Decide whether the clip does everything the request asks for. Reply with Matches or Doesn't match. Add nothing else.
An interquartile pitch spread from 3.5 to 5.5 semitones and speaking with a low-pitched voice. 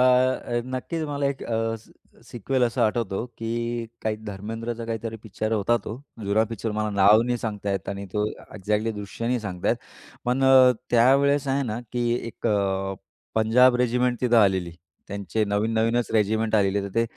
Doesn't match